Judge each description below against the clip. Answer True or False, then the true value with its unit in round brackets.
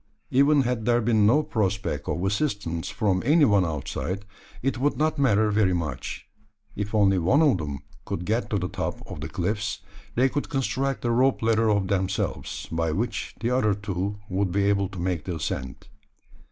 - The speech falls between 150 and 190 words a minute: True (185 wpm)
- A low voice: True (105 Hz)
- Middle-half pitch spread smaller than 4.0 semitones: False (4.8 semitones)